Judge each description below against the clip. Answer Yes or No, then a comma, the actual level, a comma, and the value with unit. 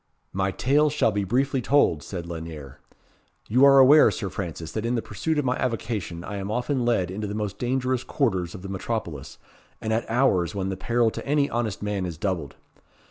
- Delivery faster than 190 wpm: Yes, average, 200 wpm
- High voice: No, low, 105 Hz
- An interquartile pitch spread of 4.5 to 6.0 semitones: Yes, average, 5.2 semitones